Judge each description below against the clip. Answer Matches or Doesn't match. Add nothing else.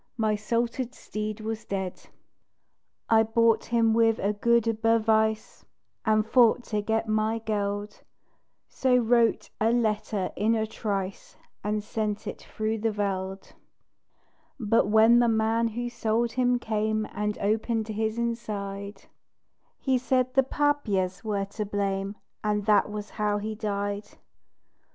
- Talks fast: Doesn't match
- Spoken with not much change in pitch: Matches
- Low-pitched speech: Doesn't match